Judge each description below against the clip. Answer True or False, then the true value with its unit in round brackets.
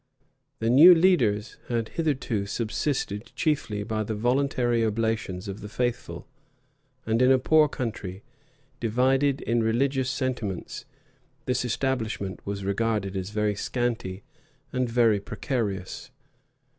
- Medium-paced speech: False (120 wpm)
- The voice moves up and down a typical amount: True (3.8 semitones)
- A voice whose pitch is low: True (115 Hz)